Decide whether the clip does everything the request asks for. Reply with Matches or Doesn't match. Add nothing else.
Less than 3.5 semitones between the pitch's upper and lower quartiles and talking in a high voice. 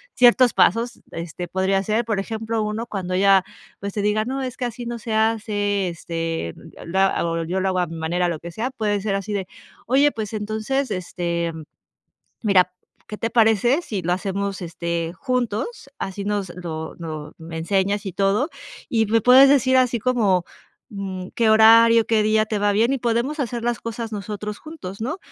Doesn't match